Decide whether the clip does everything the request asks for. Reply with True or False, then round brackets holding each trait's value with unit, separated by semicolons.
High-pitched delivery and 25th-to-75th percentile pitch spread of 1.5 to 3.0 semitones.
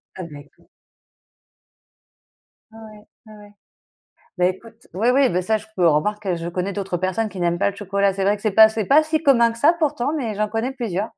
False (210 Hz; 3.6 semitones)